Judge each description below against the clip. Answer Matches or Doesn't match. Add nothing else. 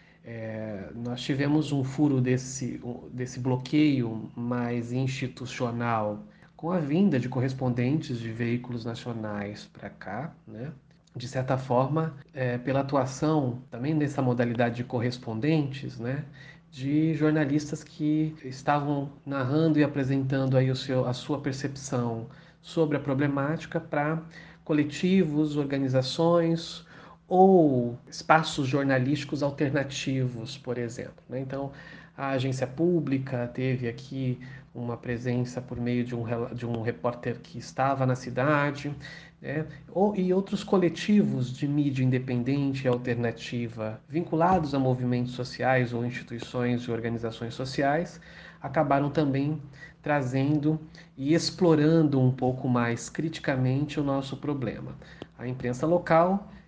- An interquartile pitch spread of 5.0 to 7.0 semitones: Doesn't match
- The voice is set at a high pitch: Doesn't match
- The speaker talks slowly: Matches